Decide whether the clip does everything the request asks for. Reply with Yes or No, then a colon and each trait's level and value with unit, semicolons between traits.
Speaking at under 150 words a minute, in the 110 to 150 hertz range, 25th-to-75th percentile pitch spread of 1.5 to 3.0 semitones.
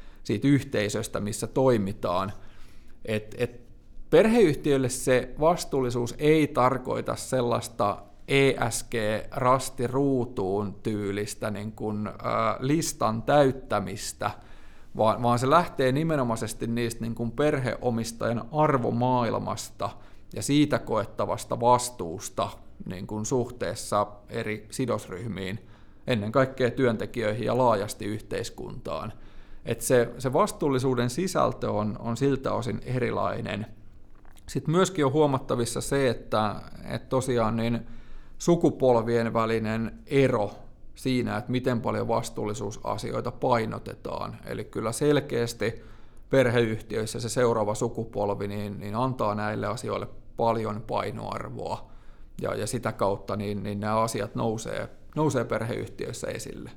No: average, 100 wpm; low, 115 Hz; average, 3.6 semitones